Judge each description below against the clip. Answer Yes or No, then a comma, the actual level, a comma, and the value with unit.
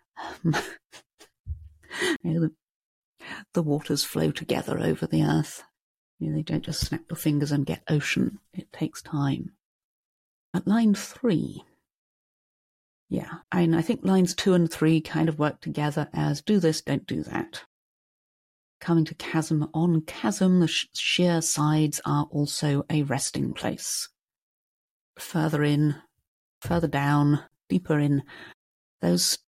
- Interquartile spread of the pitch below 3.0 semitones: Yes, narrow, 2.4 semitones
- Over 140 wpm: No, slow, 135 wpm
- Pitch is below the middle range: No, medium, 155 Hz